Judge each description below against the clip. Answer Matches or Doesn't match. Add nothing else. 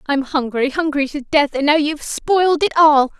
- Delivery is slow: Doesn't match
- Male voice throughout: Doesn't match